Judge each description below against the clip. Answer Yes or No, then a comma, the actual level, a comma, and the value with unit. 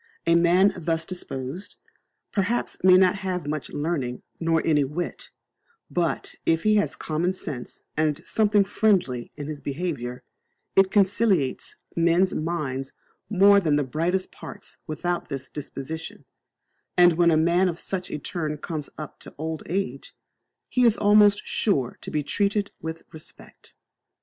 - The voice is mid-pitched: Yes, medium, 170 Hz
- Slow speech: No, average, 145 wpm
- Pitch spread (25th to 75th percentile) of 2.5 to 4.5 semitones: Yes, average, 4.1 semitones